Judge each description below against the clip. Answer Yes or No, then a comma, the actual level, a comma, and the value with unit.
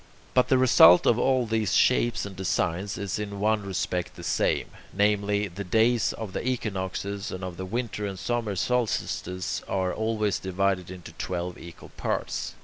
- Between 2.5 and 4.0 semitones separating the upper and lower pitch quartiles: Yes, average, 3.2 semitones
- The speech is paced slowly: No, average, 165 wpm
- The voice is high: No, low, 100 Hz